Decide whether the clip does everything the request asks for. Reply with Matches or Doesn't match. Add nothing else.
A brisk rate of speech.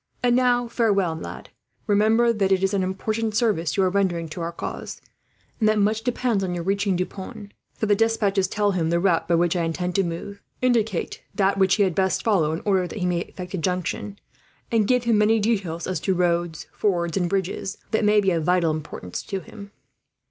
Matches